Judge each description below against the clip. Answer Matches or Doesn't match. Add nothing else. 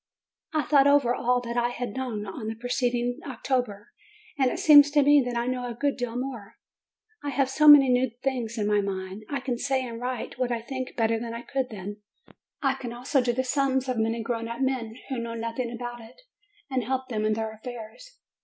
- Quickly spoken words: Matches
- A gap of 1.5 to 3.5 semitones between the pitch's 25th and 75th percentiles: Matches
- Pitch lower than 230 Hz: Doesn't match